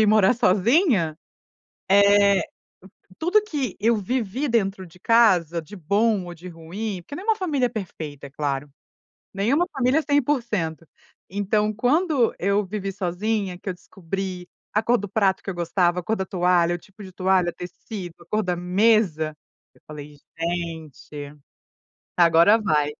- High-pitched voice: Yes, high, 195 Hz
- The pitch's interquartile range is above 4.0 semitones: Yes, average, 4.4 semitones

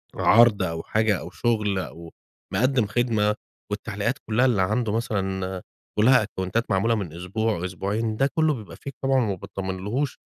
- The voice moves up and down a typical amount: Yes, average, 3.6 semitones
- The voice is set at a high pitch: No, low, 105 Hz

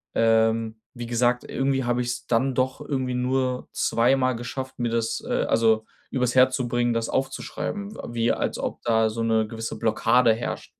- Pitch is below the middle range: Yes, low, 120 Hz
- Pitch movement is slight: Yes, narrow, 2.1 semitones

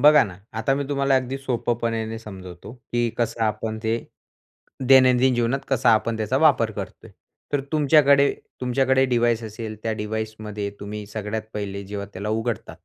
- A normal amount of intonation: Yes, average, 3.4 semitones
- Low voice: Yes, low, 115 Hz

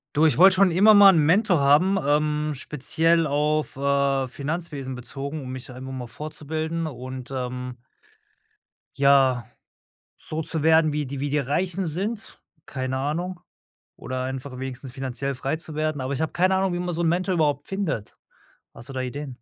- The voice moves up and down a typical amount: Yes, average, 3.8 semitones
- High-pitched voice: No, medium, 145 Hz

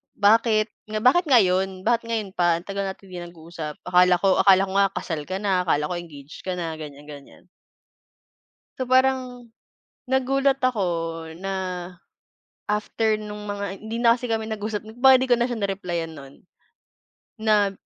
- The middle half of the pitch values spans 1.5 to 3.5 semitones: No, average, 4.6 semitones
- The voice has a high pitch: Yes, high, 200 Hz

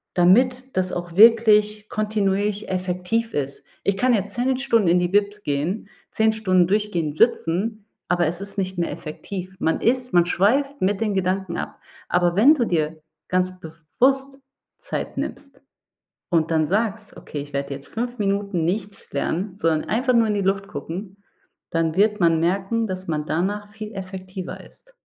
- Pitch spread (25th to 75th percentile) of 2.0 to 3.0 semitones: No, average, 3.7 semitones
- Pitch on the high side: Yes, high, 195 Hz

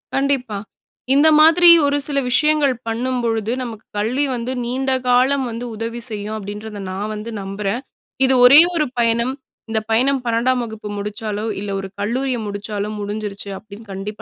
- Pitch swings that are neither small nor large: Yes, average, 3.7 semitones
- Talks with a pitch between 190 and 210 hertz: No, high, 230 Hz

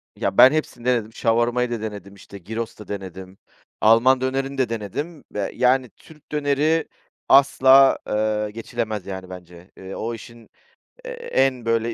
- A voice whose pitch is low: Yes, low, 115 Hz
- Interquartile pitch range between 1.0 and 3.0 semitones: No, average, 4.2 semitones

